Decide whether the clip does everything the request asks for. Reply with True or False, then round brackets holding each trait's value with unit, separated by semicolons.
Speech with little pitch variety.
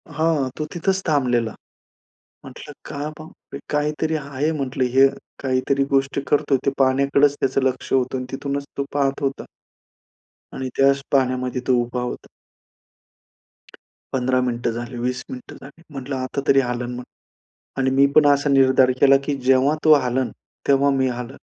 True (1.7 semitones)